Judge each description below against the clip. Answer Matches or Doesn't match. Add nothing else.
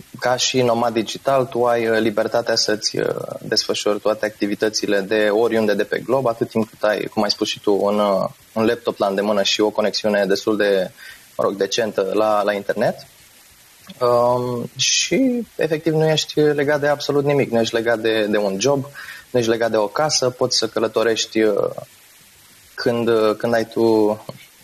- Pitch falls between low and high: Doesn't match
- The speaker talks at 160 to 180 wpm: Matches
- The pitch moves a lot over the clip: Doesn't match